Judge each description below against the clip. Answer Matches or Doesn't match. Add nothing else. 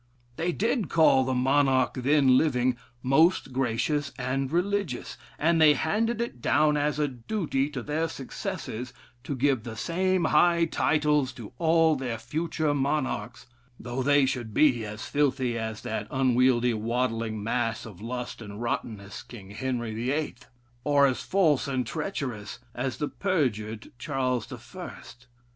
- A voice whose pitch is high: Doesn't match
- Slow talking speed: Doesn't match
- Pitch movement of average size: Matches